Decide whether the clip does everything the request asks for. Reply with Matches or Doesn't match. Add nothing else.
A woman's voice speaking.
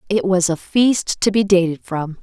Matches